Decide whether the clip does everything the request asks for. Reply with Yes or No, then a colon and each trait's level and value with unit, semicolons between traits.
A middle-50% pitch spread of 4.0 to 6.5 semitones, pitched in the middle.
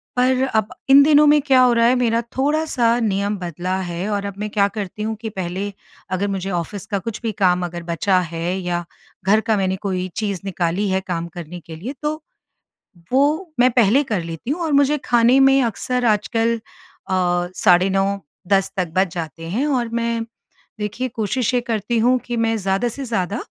No: average, 4.7 semitones; high, 210 Hz